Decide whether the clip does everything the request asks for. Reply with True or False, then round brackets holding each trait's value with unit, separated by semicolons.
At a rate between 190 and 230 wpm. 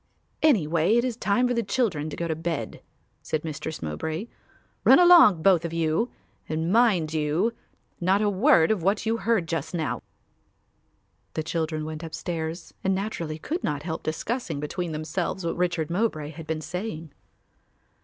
False (165 wpm)